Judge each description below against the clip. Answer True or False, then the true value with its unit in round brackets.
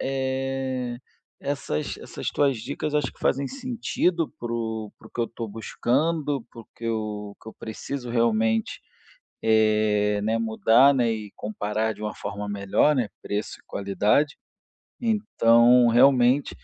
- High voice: False (115 Hz)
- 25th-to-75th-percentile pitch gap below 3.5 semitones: False (3.9 semitones)